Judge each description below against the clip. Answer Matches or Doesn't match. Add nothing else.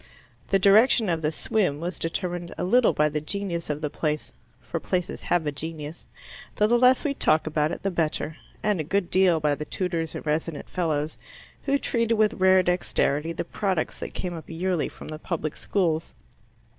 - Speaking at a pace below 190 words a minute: Doesn't match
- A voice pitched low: Doesn't match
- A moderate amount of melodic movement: Matches